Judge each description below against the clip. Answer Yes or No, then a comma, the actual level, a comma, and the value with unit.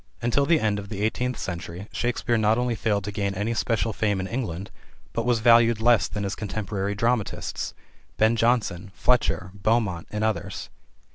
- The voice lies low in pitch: Yes, low, 110 Hz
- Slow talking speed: No, average, 170 wpm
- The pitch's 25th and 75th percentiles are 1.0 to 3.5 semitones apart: Yes, average, 2.7 semitones